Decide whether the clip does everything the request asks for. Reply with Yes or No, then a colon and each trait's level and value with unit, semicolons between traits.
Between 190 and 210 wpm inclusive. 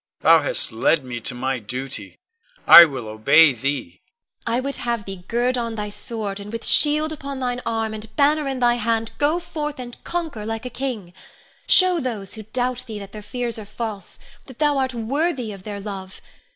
Yes: average, 200 wpm